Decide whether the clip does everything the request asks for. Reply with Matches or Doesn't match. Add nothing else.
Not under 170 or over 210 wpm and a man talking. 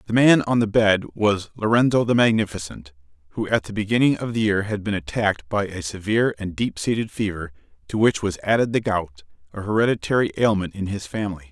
Matches